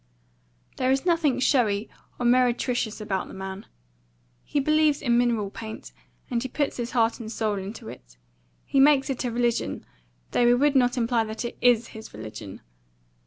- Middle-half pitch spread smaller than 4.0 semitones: Yes, average, 3.1 semitones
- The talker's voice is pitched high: Yes, high, 240 Hz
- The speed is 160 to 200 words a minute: Yes, average, 170 wpm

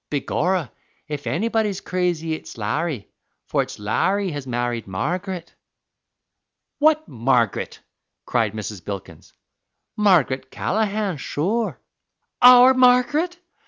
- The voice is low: No, medium, 170 Hz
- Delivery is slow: Yes, slow, 95 wpm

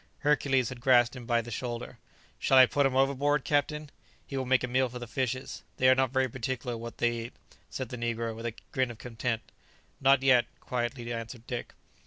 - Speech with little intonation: Yes, narrow, 2.0 semitones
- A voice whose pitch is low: Yes, low, 125 Hz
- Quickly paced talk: Yes, fast, 210 wpm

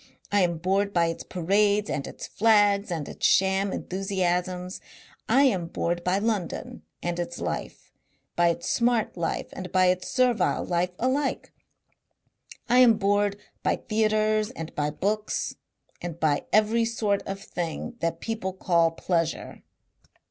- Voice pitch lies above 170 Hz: Yes, high, 190 Hz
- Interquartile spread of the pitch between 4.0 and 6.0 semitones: No, average, 3.6 semitones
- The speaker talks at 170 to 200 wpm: No, average, 145 wpm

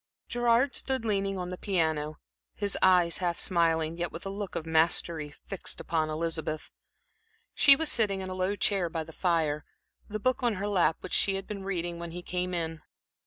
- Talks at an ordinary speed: Yes, average, 195 wpm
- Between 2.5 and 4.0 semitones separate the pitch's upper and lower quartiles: Yes, average, 3.4 semitones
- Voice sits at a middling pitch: Yes, medium, 180 Hz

